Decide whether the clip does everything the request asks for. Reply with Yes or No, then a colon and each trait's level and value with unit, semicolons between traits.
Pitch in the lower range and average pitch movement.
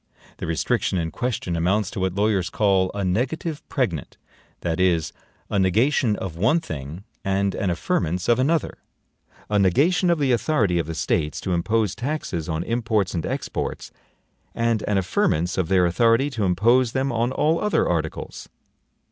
No: low, 100 Hz; wide, 5.7 semitones